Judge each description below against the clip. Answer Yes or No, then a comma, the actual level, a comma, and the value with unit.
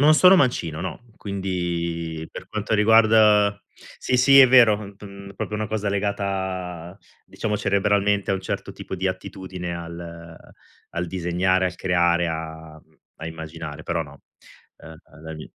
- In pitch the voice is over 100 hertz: No, very low, 95 Hz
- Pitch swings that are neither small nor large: Yes, average, 3.5 semitones